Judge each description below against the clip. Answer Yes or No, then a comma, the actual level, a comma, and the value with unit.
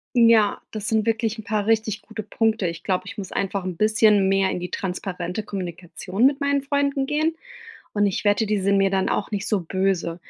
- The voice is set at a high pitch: Yes, high, 205 Hz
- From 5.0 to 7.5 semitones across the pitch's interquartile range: No, average, 2.7 semitones